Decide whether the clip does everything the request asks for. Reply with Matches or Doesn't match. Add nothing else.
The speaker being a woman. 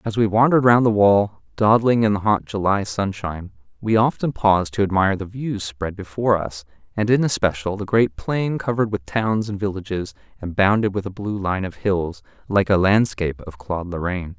Doesn't match